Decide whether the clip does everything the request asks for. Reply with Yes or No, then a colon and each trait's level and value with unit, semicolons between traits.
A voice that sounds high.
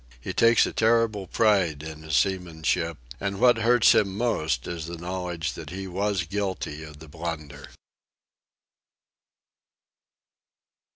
No: very low, 90 Hz